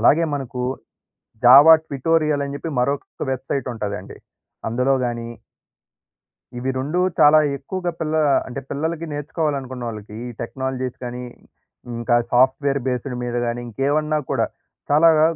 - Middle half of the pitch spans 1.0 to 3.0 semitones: No, average, 3.7 semitones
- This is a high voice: No, low, 135 Hz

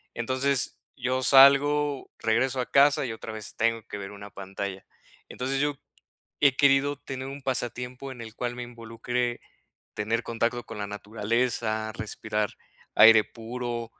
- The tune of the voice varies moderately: Yes, average, 3.1 semitones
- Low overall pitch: Yes, low, 120 Hz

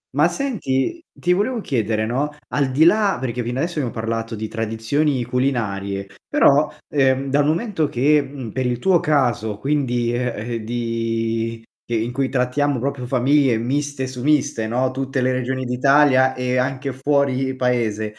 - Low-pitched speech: Yes, low, 130 Hz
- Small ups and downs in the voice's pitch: No, average, 3.4 semitones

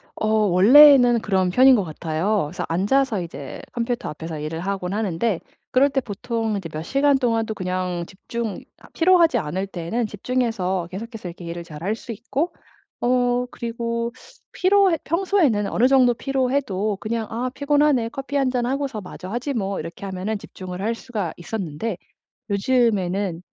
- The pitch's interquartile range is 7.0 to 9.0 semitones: No, wide, 5.4 semitones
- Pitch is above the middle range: Yes, high, 225 Hz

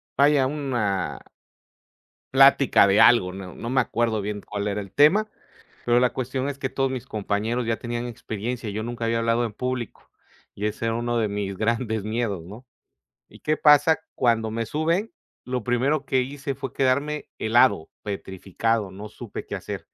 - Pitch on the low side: Yes, low, 120 Hz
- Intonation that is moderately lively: Yes, average, 3.7 semitones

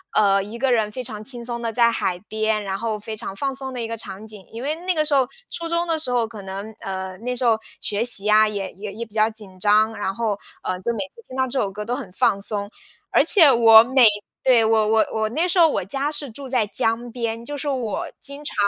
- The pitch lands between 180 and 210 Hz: No, high, 225 Hz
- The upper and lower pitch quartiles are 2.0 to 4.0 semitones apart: Yes, average, 3.6 semitones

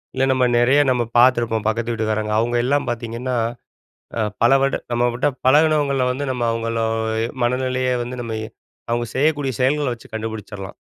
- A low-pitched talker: Yes, low, 120 Hz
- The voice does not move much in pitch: Yes, narrow, 2.3 semitones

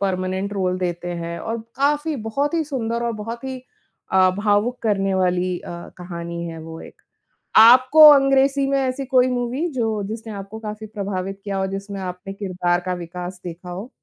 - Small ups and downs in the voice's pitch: No, average, 5.3 semitones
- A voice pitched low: No, high, 200 Hz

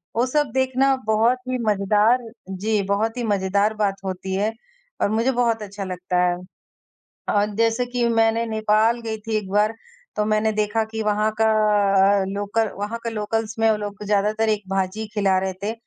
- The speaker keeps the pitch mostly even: Yes, narrow, 1.8 semitones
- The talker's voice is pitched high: Yes, high, 215 Hz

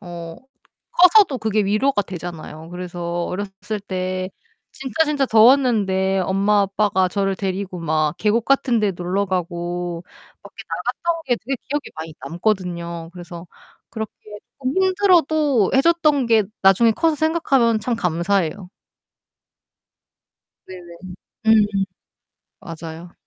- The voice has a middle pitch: No, high, 195 Hz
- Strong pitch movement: Yes, wide, 5.8 semitones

